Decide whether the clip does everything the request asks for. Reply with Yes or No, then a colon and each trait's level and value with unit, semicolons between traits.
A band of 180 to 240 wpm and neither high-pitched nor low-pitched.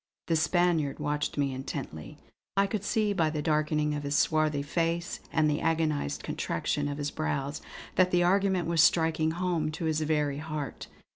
No: average, 170 wpm; medium, 155 Hz